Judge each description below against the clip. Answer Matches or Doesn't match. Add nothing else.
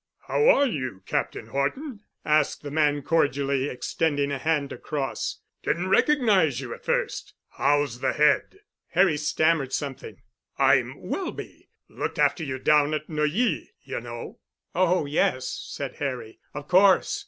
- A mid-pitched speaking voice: Matches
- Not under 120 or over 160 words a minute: Matches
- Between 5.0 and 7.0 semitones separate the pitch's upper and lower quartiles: Doesn't match